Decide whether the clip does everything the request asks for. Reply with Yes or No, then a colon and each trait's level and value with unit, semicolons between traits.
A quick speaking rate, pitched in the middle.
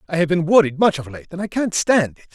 Yes: fast, 305 wpm; medium, 170 Hz